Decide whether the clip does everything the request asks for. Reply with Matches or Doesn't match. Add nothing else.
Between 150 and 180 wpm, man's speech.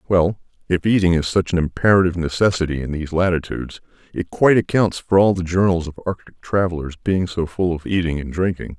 Doesn't match